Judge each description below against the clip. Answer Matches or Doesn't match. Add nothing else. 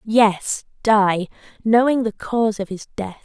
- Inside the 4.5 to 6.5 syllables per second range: Doesn't match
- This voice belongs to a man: Doesn't match